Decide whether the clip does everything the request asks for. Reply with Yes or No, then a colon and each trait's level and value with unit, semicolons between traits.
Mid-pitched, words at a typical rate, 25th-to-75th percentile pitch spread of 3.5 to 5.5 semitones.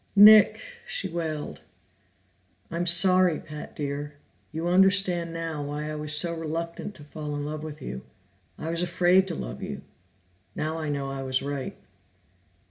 No: medium, 160 Hz; average, 155 wpm; average, 2.9 semitones